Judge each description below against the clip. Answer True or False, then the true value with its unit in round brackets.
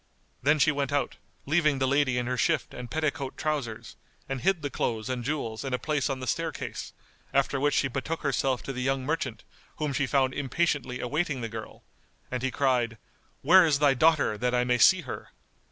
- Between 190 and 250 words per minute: True (200 wpm)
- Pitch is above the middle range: False (135 Hz)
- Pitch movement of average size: True (3.0 semitones)